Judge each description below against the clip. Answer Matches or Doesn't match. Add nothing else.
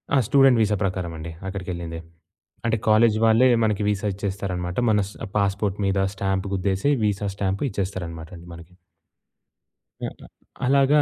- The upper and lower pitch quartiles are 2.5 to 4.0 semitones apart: Matches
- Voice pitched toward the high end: Doesn't match